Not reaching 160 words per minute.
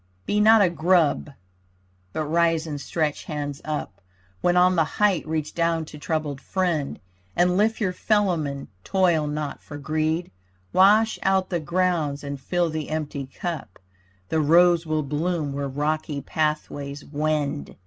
Yes: average, 150 wpm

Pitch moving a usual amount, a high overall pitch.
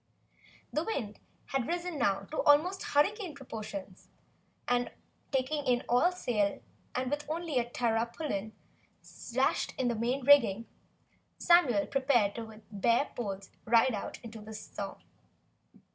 Yes: average, 4.9 semitones; high, 245 Hz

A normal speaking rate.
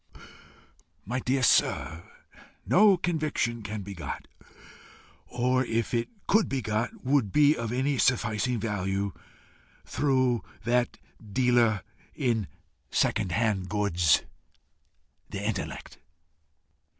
No: slow, 100 wpm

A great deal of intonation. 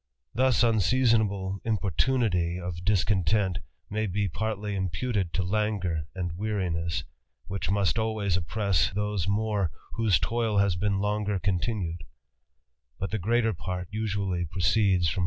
No: average, 3.2 semitones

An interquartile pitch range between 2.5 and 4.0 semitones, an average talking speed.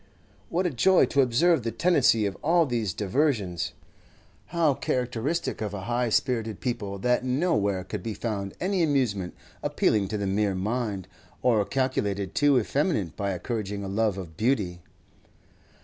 No: average, 5.2 semitones; average, 150 wpm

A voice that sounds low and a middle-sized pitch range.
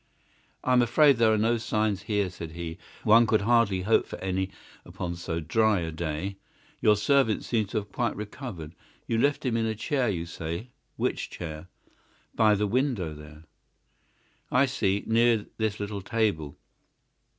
Yes: low, 105 Hz; average, 4.6 semitones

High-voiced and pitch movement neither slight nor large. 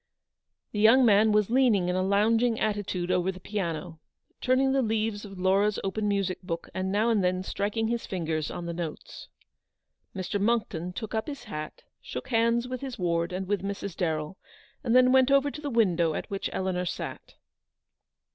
Yes: high, 200 Hz; average, 4.1 semitones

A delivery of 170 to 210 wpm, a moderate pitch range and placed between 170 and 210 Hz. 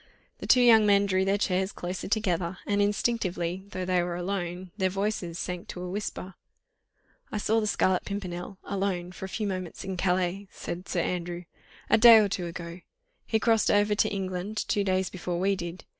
No: average, 190 wpm; narrow, 2.3 semitones; high, 190 Hz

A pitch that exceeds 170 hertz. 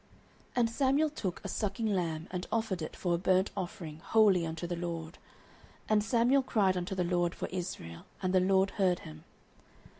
Yes: medium, 185 Hz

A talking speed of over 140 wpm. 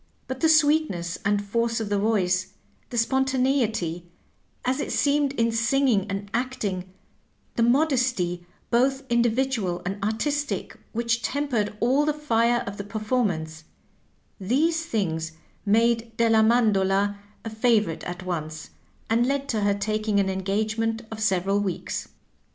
No: slow, 135 wpm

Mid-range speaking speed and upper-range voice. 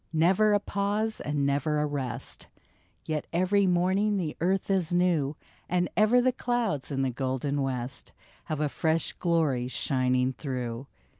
No: average, 155 wpm; medium, 155 Hz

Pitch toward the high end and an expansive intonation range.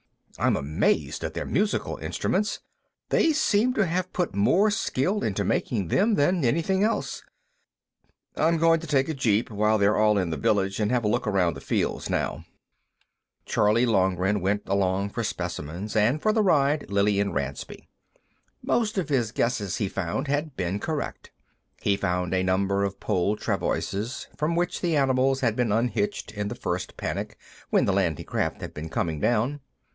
No: low, 110 Hz; wide, 7.6 semitones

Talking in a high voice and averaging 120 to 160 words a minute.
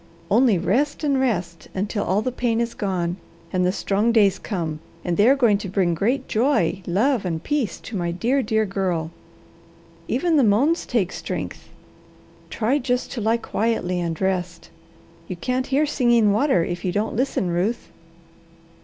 No: high, 210 Hz; average, 170 wpm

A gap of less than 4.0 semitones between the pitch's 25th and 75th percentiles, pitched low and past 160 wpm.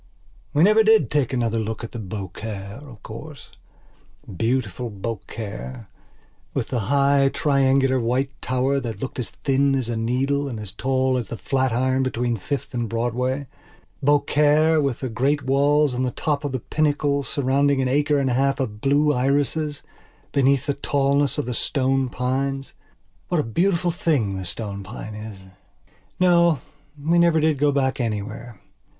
No: average, 3.4 semitones; low, 130 Hz; average, 155 wpm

